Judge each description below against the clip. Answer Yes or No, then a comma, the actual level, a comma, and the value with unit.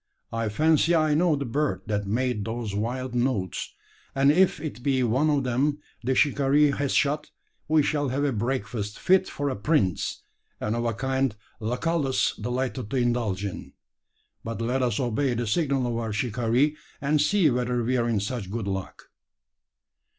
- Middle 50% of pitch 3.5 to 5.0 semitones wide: Yes, average, 3.9 semitones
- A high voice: No, low, 125 Hz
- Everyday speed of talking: Yes, average, 170 wpm